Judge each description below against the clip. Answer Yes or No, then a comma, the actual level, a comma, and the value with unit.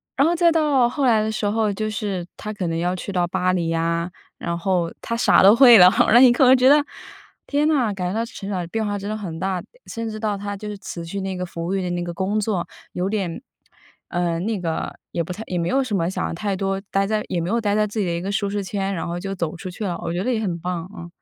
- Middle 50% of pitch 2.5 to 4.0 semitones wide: Yes, average, 3.5 semitones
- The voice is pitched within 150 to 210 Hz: Yes, high, 195 Hz